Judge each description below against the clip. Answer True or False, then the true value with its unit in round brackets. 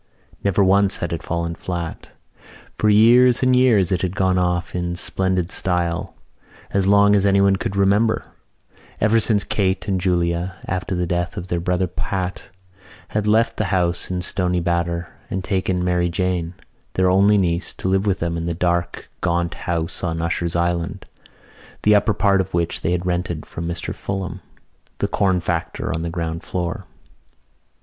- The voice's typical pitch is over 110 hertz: False (90 Hz)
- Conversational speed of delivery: True (170 wpm)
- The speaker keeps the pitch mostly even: True (2.2 semitones)